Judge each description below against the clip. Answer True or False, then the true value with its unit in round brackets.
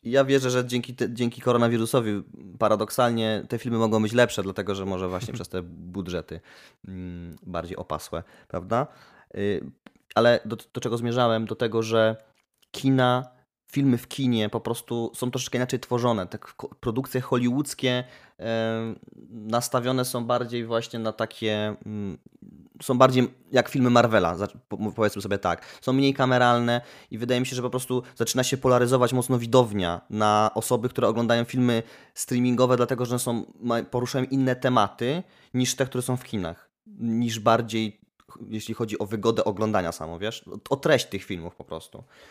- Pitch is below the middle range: True (120 Hz)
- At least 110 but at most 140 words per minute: False (155 wpm)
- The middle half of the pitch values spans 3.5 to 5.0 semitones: False (2.7 semitones)